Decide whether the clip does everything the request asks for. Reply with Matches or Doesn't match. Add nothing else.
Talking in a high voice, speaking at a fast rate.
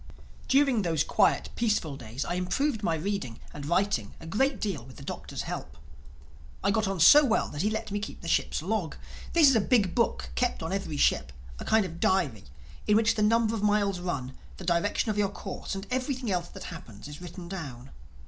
Matches